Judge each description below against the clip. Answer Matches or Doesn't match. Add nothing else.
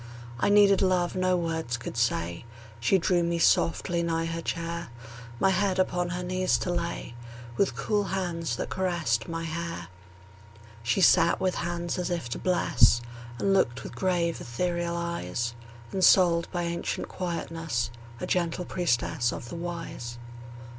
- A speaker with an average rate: Matches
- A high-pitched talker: Doesn't match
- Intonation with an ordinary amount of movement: Doesn't match